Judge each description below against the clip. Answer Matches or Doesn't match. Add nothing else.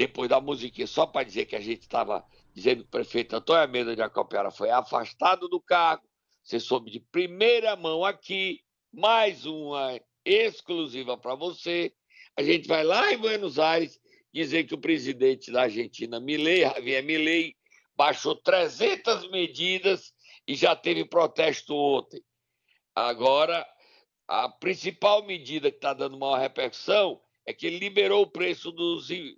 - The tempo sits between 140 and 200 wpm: Matches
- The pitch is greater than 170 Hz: Matches